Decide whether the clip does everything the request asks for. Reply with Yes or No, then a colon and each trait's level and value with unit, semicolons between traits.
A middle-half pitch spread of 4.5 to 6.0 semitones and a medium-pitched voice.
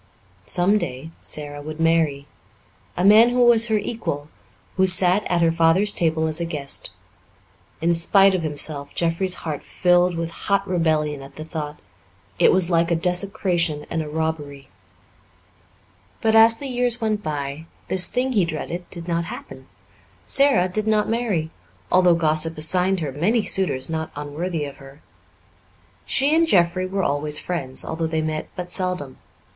No: average, 3.7 semitones; medium, 170 Hz